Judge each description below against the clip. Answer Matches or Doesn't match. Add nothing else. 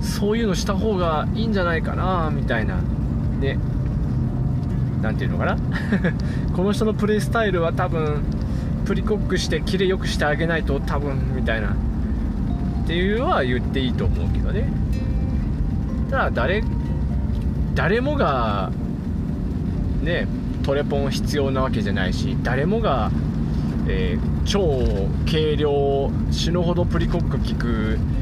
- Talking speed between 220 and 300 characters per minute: Matches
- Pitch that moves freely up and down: Matches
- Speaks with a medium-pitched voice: Doesn't match